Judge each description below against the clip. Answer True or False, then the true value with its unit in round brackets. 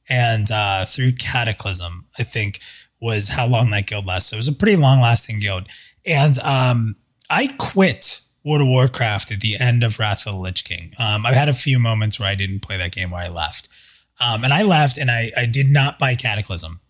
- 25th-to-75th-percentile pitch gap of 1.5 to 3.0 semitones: False (4.3 semitones)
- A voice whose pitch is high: False (115 Hz)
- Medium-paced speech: False (220 wpm)